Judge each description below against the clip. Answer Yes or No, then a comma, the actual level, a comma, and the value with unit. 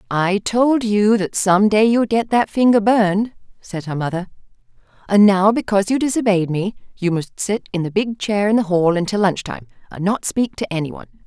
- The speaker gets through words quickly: Yes, fast, 210 wpm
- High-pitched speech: Yes, high, 200 Hz